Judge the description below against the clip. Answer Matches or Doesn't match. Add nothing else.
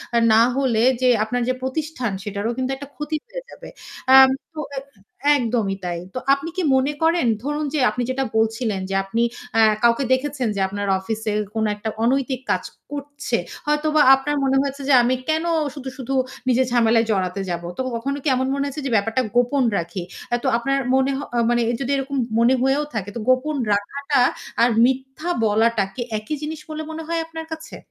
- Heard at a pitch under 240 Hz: Doesn't match